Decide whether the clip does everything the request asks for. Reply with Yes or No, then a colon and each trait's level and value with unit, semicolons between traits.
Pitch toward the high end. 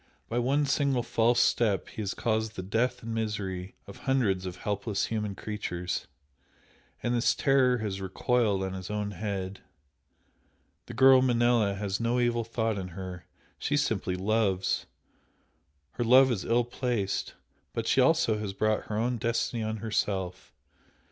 No: low, 110 Hz